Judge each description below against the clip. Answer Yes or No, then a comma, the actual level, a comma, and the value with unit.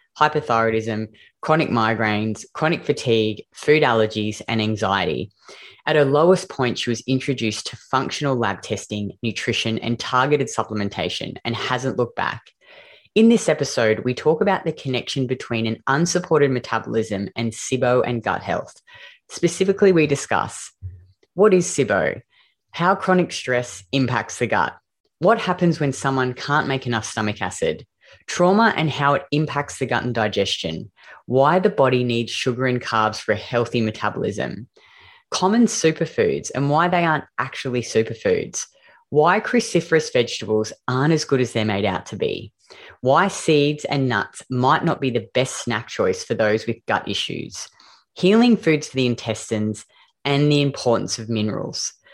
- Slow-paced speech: No, average, 150 wpm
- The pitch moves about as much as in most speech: No, wide, 5.7 semitones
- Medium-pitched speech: No, low, 130 Hz